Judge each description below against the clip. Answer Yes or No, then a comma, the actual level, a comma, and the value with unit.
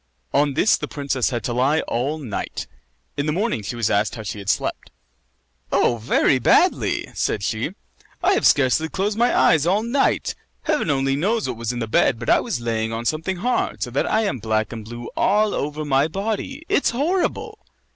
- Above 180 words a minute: Yes, average, 200 wpm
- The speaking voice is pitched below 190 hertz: Yes, medium, 140 Hz